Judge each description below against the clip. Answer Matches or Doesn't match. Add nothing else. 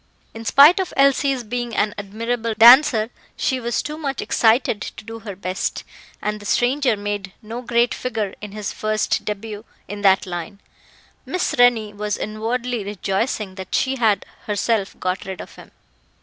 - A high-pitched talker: Matches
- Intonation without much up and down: Doesn't match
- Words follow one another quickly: Doesn't match